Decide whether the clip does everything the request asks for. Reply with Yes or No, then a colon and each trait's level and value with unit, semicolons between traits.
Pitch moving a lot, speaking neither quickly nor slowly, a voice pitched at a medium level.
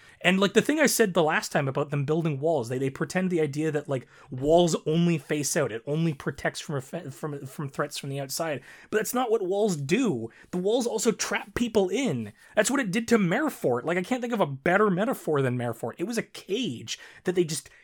No: wide, 6.6 semitones; fast, 235 wpm; medium, 165 Hz